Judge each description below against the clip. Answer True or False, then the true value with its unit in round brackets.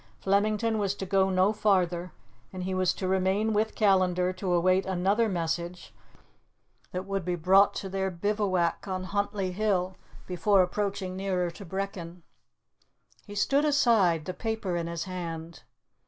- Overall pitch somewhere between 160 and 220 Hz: True (190 Hz)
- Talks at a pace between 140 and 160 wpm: True (150 wpm)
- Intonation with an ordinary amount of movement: False (2.1 semitones)